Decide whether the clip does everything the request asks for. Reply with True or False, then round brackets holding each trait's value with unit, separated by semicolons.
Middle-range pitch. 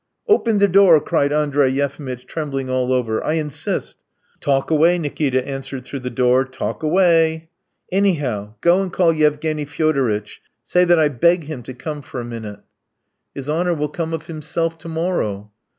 True (150 Hz)